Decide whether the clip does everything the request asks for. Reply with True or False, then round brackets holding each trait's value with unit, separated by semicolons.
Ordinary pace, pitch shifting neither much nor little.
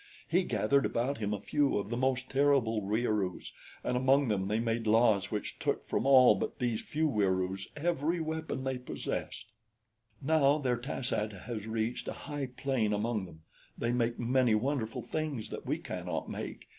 True (175 wpm; 4.4 semitones)